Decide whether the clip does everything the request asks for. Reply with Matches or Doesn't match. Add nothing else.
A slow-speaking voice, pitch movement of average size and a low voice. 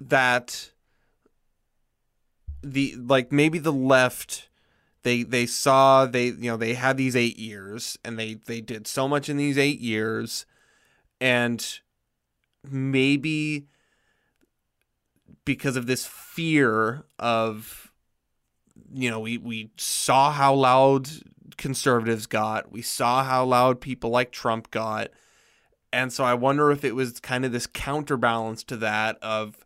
Matches